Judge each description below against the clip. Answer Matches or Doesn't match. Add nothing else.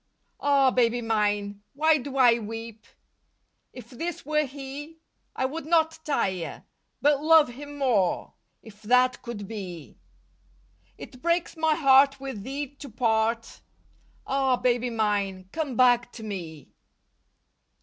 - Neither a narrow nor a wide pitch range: Matches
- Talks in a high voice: Matches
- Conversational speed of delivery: Doesn't match